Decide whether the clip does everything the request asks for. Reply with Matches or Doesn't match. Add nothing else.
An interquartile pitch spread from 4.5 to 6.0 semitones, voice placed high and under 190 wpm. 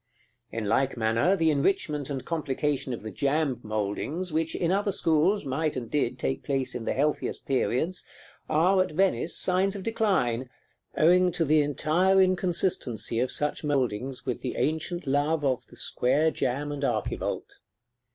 Doesn't match